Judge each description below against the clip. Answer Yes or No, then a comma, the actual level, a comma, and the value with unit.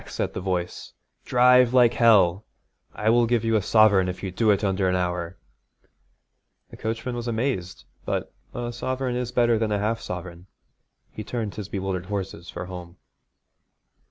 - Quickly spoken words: No, average, 165 wpm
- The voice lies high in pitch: No, low, 105 Hz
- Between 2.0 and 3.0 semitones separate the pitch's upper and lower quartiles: No, average, 4.3 semitones